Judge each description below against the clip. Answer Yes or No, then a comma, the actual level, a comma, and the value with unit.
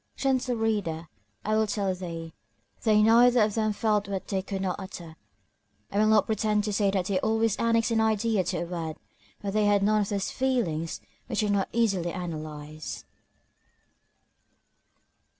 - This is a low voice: No, high, 205 Hz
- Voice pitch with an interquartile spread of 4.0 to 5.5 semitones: No, average, 3.3 semitones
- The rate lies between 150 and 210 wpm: Yes, average, 170 wpm